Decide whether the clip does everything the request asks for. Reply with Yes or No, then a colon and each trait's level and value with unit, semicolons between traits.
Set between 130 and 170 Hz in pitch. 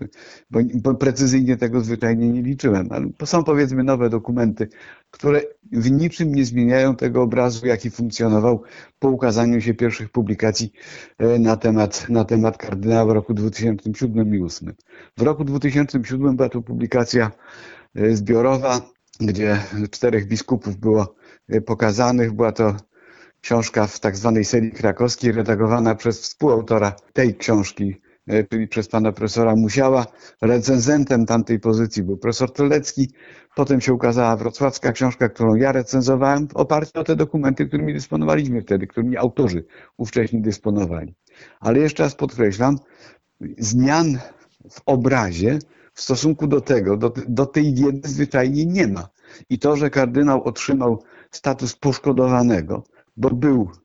No: low, 120 Hz